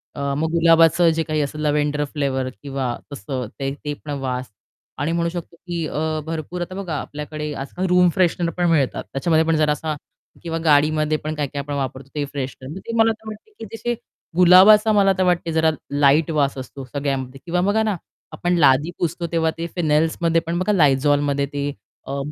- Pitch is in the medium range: Yes, medium, 155 Hz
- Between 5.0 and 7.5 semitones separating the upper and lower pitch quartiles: No, average, 3.2 semitones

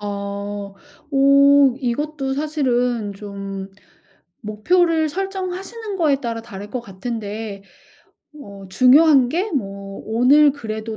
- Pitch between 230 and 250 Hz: Yes, high, 245 Hz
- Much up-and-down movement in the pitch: Yes, wide, 6.3 semitones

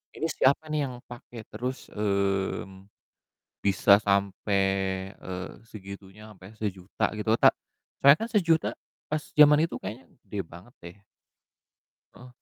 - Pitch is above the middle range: No, low, 105 Hz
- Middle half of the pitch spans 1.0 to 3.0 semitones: No, average, 5.3 semitones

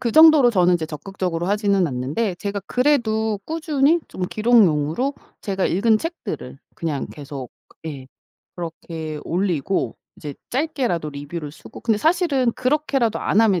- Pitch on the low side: No, high, 200 Hz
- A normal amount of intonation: No, wide, 7.6 semitones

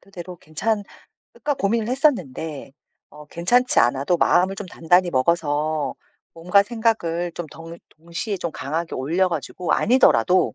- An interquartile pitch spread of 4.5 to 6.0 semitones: No, average, 4.0 semitones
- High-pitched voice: No, medium, 175 Hz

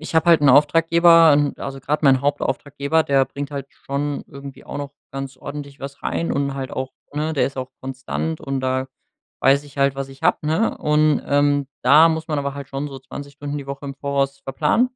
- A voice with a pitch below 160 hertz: Yes, medium, 140 Hz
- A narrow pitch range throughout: Yes, narrow, 1.6 semitones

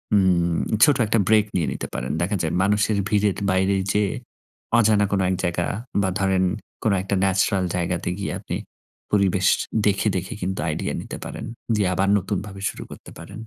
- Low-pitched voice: Yes, very low, 95 Hz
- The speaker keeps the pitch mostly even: Yes, narrow, 2.0 semitones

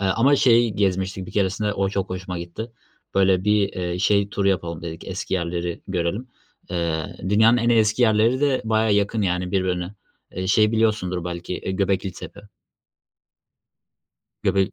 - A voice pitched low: Yes, very low, 95 Hz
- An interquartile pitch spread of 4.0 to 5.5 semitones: No, average, 2.9 semitones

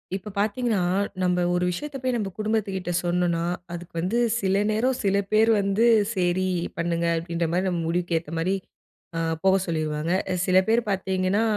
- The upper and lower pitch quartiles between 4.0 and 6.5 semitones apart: No, average, 3.4 semitones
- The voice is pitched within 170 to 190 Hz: Yes, medium, 185 Hz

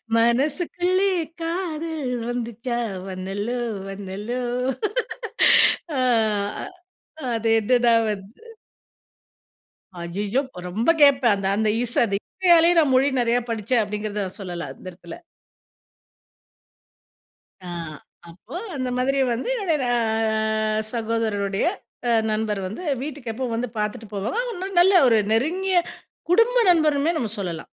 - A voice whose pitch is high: Yes, high, 235 Hz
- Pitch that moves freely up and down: Yes, wide, 5.7 semitones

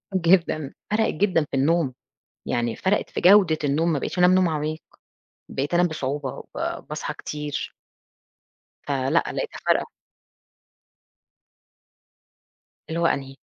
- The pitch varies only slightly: No, average, 4.1 semitones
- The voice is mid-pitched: Yes, medium, 155 Hz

